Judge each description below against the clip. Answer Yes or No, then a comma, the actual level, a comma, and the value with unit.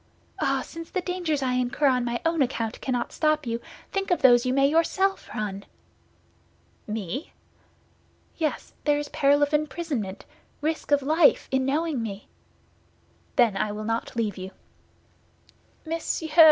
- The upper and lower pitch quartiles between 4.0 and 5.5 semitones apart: Yes, average, 5.1 semitones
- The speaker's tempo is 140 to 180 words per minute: Yes, average, 145 wpm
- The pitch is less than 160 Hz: No, very high, 275 Hz